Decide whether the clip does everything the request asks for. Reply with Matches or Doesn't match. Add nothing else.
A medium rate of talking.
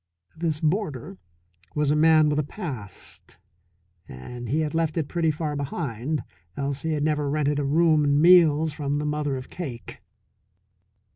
Matches